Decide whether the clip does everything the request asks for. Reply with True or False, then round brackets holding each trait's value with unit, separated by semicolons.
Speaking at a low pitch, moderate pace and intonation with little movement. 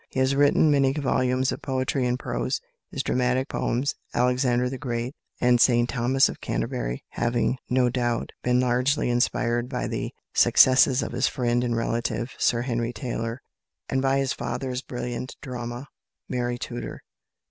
True (125 Hz; 155 wpm; 1.5 semitones)